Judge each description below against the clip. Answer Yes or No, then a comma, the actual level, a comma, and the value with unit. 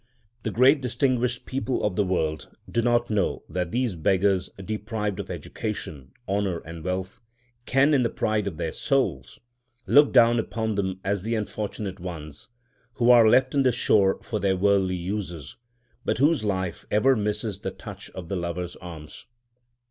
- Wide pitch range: No, average, 4.6 semitones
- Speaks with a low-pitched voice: Yes, low, 105 Hz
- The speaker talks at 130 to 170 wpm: Yes, average, 160 wpm